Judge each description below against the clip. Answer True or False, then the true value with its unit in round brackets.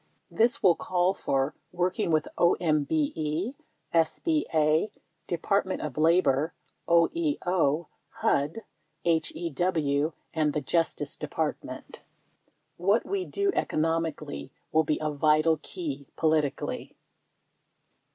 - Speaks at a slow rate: True (95 wpm)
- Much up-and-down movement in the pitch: False (2.9 semitones)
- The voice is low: False (160 Hz)